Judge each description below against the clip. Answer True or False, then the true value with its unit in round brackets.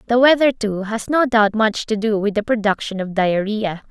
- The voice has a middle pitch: False (215 Hz)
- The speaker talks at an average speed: False (215 wpm)